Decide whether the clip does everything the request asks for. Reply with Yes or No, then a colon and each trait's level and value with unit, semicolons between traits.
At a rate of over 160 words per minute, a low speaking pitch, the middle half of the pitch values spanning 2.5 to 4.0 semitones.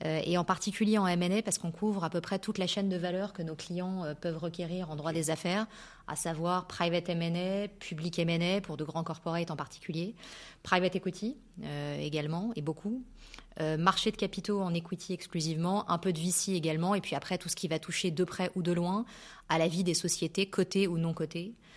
No: average, 205 wpm; medium, 180 Hz; average, 2.8 semitones